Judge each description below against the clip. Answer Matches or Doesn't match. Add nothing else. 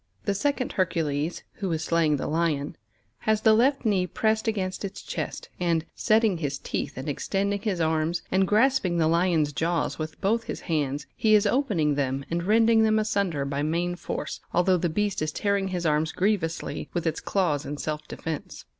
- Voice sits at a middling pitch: Matches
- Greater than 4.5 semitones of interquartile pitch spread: Matches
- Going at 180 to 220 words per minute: Matches